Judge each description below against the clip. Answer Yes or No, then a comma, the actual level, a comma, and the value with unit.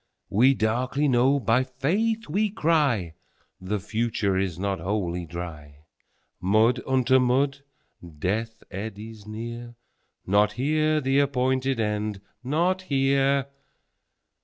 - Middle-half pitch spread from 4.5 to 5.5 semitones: Yes, average, 4.9 semitones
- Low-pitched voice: Yes, low, 120 Hz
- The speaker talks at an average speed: No, slow, 100 wpm